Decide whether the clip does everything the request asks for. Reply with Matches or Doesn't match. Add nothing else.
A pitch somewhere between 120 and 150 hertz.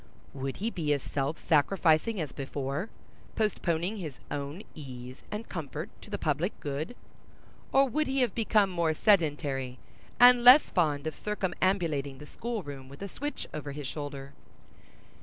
Doesn't match